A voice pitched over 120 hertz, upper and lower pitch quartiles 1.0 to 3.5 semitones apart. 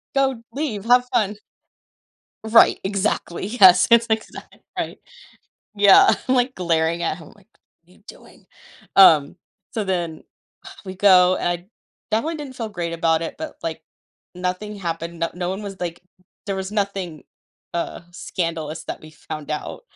No: medium, 185 Hz; average, 4.1 semitones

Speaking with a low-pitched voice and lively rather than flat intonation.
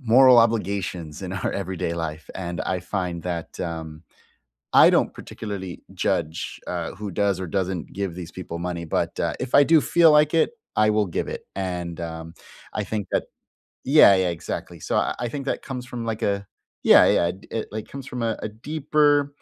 Yes: low, 100 Hz; wide, 5.8 semitones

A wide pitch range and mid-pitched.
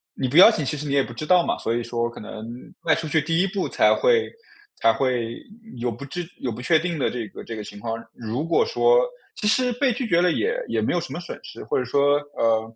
Yes: wide, 7.5 semitones; medium, 145 Hz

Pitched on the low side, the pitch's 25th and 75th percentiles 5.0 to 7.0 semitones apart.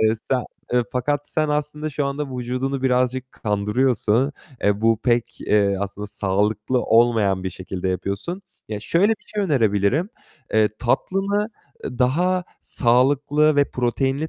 Yes: low, 125 Hz; wide, 5.6 semitones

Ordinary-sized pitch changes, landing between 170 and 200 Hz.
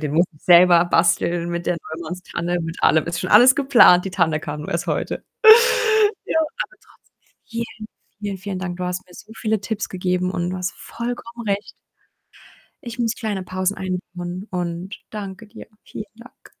Yes: average, 3.6 semitones; medium, 185 Hz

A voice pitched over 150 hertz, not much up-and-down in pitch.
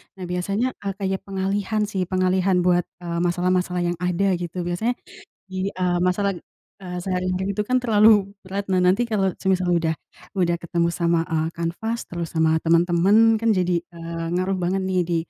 Yes: medium, 185 Hz; narrow, 2.1 semitones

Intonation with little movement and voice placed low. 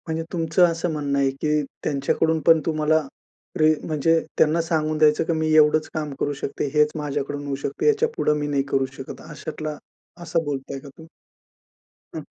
No: narrow, 1.8 semitones; medium, 155 Hz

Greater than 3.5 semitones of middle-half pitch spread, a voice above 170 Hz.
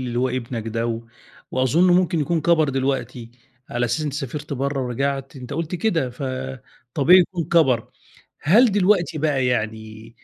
No: average, 4.7 semitones; low, 135 Hz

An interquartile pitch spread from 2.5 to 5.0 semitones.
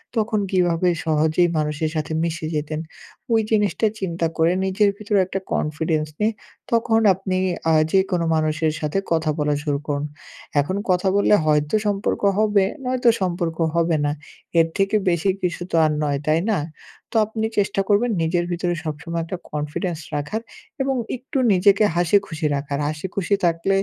Yes: average, 4.4 semitones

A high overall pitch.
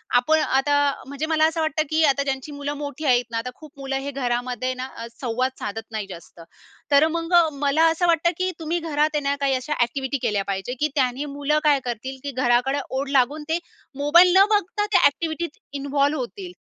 Yes: very high, 280 Hz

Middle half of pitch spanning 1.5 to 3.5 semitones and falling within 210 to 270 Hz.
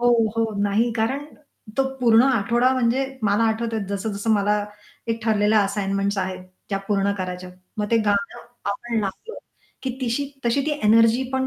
Yes: average, 3.0 semitones; high, 220 Hz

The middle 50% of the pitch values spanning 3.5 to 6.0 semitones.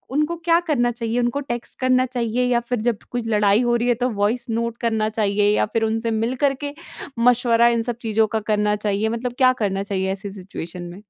No: average, 2.7 semitones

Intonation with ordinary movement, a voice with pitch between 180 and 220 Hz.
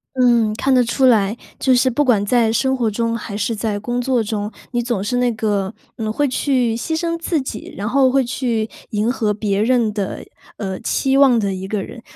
No: average, 3.3 semitones; high, 230 Hz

